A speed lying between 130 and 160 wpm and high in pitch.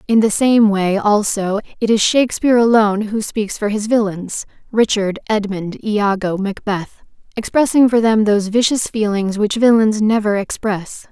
Yes: average, 150 wpm; high, 215 Hz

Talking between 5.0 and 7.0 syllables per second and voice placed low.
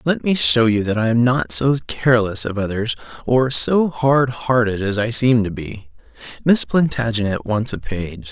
No: 4.5 syllables/s; low, 115 Hz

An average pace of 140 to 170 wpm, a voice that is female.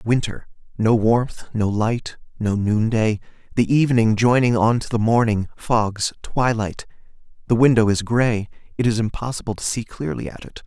No: average, 160 wpm; male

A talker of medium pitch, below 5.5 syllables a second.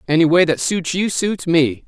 Yes: medium, 170 Hz; 4.7 syllables/s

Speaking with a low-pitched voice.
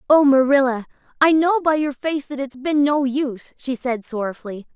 No: very high, 275 Hz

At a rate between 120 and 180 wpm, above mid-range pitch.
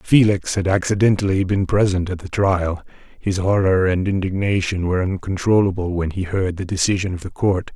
No: average, 170 wpm; very low, 95 Hz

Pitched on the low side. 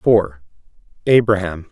Yes: low, 105 Hz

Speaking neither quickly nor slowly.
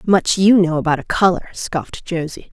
Yes: average, 185 wpm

